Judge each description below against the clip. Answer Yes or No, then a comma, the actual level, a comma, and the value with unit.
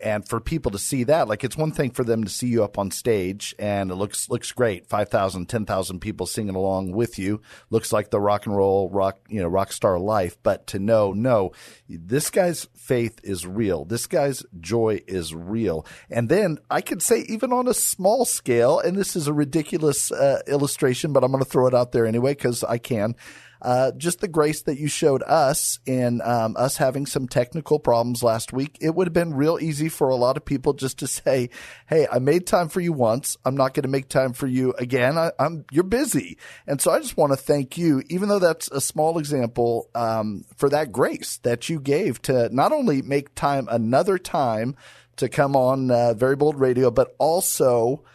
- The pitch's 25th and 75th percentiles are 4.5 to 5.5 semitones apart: Yes, average, 4.8 semitones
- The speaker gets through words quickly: Yes, fast, 215 wpm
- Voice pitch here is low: Yes, low, 130 Hz